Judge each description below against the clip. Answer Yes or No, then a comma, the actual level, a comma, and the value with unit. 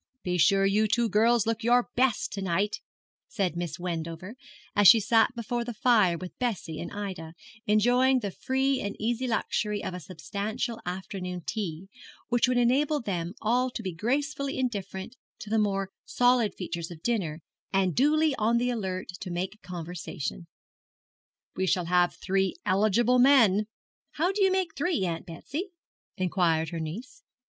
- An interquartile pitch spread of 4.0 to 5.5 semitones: Yes, average, 5.1 semitones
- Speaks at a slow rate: No, average, 160 wpm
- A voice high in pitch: Yes, high, 210 Hz